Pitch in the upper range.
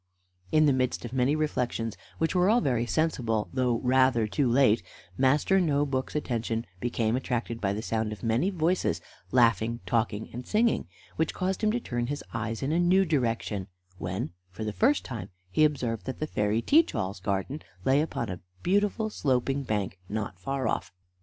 No: low, 125 Hz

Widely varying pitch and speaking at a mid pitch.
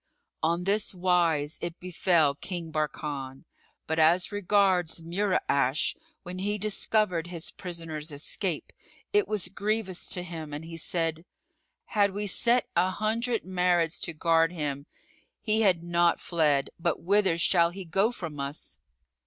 No: average, 3.3 semitones; medium, 175 Hz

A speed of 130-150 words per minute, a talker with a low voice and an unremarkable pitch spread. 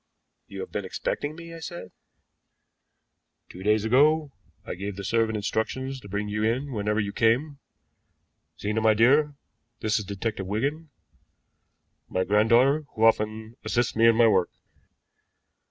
Yes: average, 145 wpm; low, 110 Hz; average, 4.5 semitones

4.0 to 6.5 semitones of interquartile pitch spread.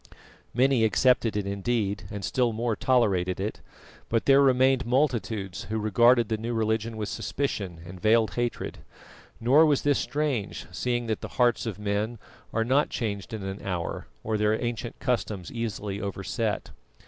No: average, 3.1 semitones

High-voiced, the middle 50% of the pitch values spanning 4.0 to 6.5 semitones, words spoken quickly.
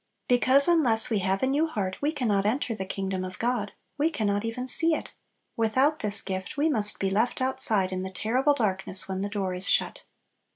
Yes: high, 220 Hz; average, 5.2 semitones; fast, 215 wpm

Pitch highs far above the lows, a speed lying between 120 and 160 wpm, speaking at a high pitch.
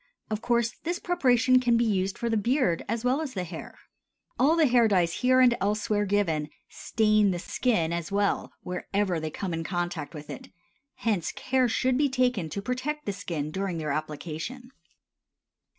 No: wide, 6.3 semitones; average, 180 wpm; high, 210 Hz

